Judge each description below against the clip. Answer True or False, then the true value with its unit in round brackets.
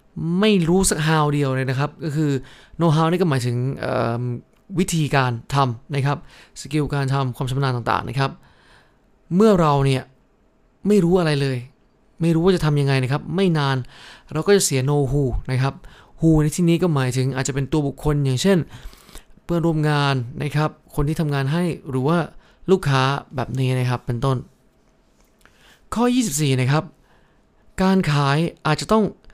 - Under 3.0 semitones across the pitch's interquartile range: False (3.8 semitones)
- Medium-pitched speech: True (145 Hz)